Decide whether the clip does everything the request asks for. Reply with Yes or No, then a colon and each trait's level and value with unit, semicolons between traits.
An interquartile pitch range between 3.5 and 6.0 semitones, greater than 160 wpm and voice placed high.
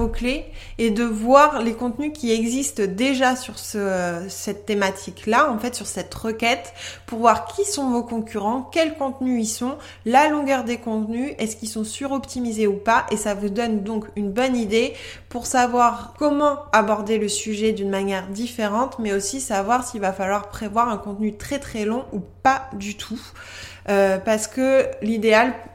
No: average, 3.0 semitones; average, 180 wpm; high, 230 Hz